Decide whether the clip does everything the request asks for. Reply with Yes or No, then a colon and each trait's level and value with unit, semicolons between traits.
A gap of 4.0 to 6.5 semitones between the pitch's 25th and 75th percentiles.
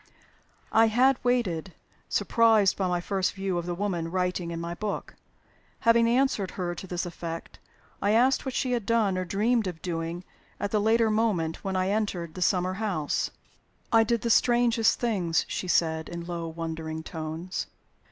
Yes: average, 4.7 semitones